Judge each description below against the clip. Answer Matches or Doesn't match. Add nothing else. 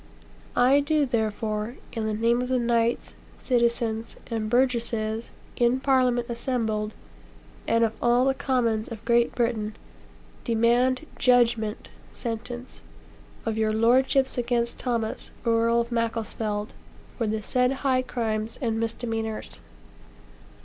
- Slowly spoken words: Matches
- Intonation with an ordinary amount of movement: Doesn't match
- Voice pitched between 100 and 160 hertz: Doesn't match